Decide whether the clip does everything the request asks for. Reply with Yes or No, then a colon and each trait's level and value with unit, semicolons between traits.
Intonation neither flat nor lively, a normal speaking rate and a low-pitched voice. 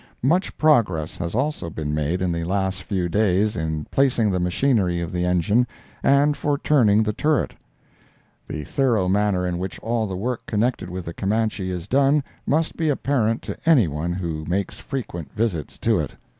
No: wide, 6.1 semitones; average, 175 wpm; low, 100 Hz